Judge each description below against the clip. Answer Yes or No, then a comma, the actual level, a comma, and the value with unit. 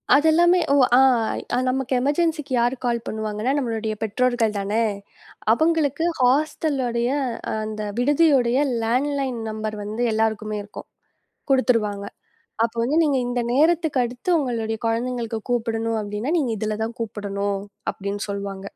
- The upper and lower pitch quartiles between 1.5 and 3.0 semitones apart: No, average, 3.8 semitones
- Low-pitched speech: No, high, 235 Hz